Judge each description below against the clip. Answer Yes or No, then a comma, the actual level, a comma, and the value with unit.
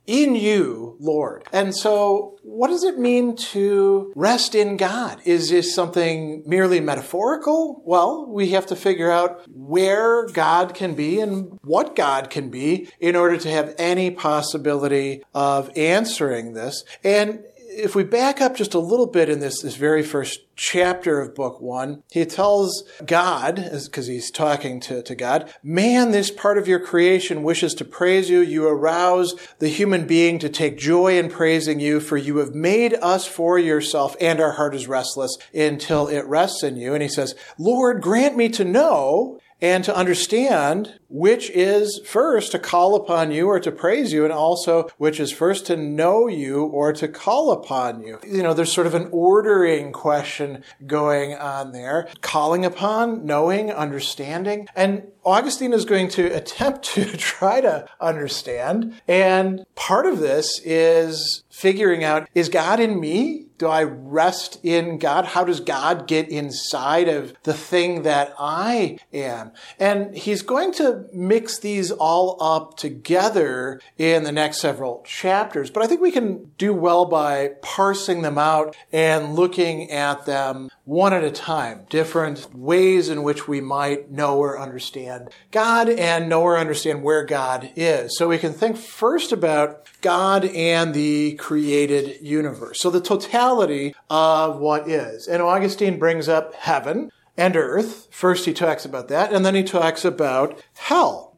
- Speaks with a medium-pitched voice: Yes, medium, 170 Hz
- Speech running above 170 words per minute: No, average, 165 wpm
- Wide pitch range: No, average, 4.6 semitones